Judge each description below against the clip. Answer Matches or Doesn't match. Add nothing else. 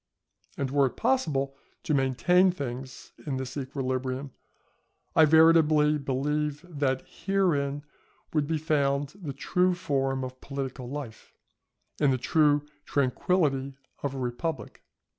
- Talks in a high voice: Doesn't match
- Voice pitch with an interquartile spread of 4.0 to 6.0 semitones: Doesn't match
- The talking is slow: Matches